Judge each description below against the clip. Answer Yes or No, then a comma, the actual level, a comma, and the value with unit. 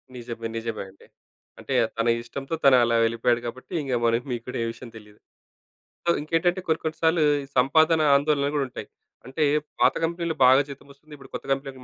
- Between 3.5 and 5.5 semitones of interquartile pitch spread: Yes, average, 4.8 semitones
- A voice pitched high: No, low, 135 Hz